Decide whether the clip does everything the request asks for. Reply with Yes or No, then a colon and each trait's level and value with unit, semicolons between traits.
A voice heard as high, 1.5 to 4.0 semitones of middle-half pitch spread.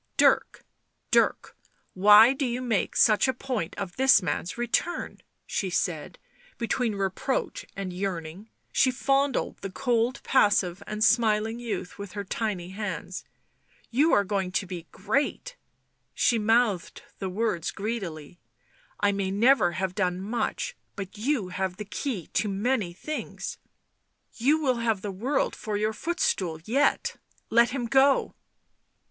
No: high, 210 Hz; average, 4.6 semitones